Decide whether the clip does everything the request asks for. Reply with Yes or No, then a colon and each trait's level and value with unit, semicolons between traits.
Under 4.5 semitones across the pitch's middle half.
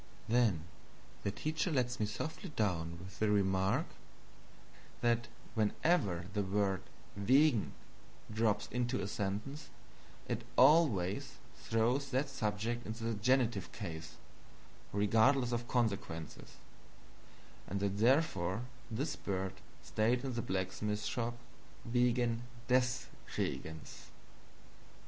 Yes: average, 4.0 semitones